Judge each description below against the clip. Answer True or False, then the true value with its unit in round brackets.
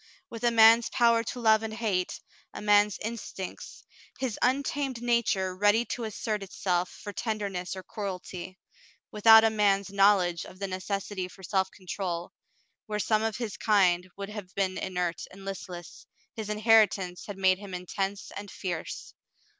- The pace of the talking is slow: False (155 wpm)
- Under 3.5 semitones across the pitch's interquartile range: True (2.9 semitones)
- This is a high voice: True (200 Hz)